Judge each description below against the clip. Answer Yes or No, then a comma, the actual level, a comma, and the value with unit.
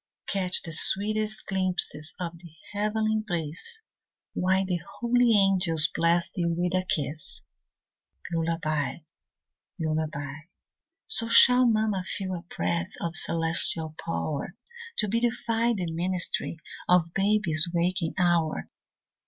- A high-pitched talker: No, medium, 180 Hz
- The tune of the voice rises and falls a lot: No, average, 4.3 semitones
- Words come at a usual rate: No, slow, 110 wpm